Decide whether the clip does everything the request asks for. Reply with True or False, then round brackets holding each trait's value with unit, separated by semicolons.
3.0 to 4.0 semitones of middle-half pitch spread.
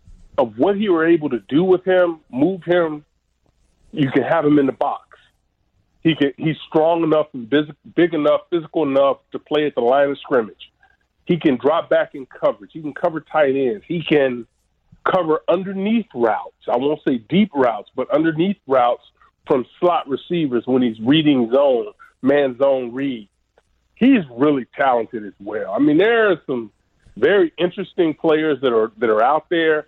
False (4.7 semitones)